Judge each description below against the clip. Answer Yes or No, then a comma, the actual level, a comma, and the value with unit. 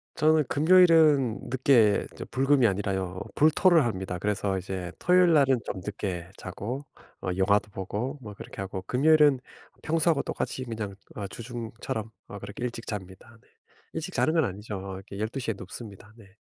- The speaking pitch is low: Yes, low, 115 Hz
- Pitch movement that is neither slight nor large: No, wide, 6.2 semitones